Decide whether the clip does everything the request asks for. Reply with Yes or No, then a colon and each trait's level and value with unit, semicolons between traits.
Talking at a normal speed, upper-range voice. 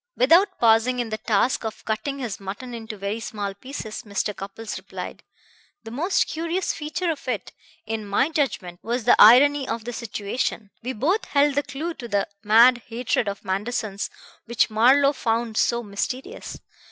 Yes: average, 165 wpm; high, 235 Hz